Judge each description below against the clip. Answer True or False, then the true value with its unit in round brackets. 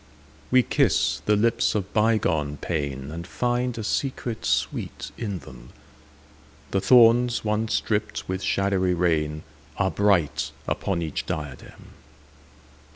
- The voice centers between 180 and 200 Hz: False (95 Hz)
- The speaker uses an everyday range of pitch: False (6.3 semitones)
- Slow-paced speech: True (105 wpm)